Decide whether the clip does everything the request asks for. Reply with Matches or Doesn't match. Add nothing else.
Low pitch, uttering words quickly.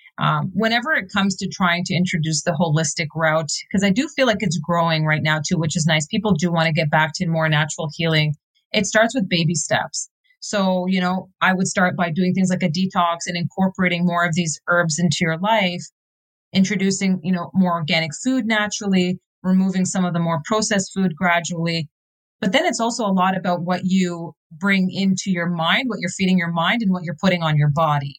Doesn't match